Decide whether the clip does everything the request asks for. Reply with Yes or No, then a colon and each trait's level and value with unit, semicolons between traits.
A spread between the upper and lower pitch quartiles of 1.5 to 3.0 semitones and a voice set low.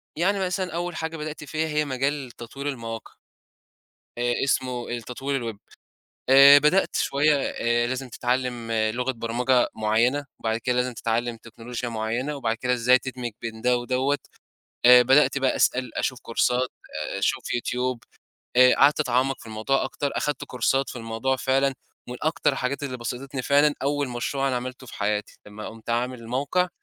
Yes: average, 2.7 semitones; low, 125 Hz